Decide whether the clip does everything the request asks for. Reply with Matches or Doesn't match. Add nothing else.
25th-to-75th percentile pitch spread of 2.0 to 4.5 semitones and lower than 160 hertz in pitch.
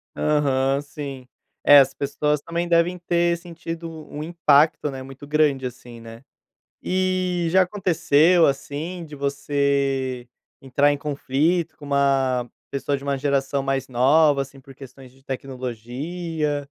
Matches